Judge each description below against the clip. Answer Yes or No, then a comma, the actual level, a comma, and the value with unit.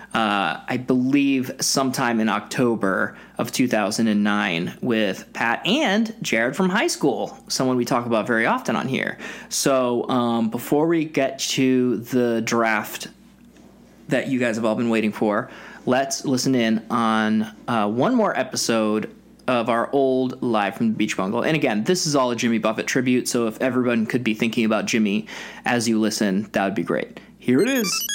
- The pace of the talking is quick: No, average, 175 wpm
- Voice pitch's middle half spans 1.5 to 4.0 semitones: Yes, average, 3.3 semitones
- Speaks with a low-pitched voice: Yes, low, 120 Hz